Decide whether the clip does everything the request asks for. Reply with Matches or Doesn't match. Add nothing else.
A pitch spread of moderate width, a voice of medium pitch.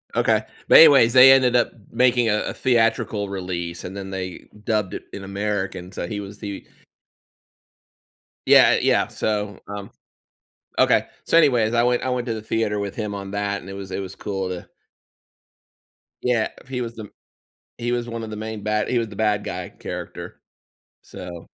Doesn't match